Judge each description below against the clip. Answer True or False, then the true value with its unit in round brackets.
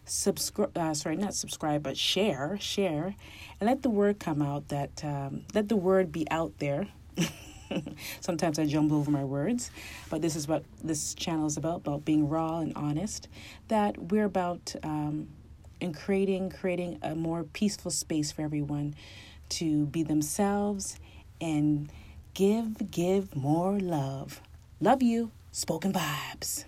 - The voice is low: False (160 Hz)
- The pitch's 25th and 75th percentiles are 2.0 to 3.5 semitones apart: False (4.7 semitones)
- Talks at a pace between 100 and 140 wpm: False (150 wpm)